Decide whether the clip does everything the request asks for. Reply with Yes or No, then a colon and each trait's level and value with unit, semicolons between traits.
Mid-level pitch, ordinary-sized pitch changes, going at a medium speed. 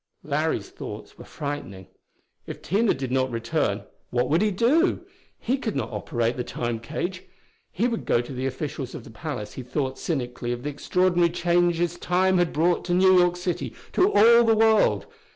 No: medium, 170 Hz; wide, 6.5 semitones; average, 185 wpm